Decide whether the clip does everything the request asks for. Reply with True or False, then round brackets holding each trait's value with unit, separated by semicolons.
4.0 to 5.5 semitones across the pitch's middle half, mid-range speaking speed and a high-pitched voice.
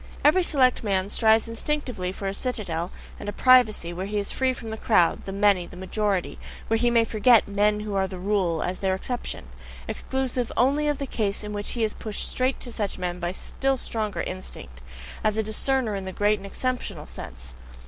False (4.3 semitones; 210 wpm; 210 Hz)